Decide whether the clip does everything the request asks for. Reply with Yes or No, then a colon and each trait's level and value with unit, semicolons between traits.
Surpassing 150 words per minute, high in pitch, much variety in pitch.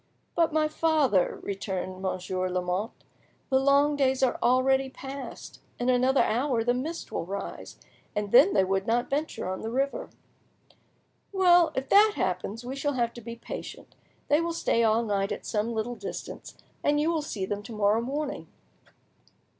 Yes: average, 170 wpm; high, 245 Hz; wide, 5.7 semitones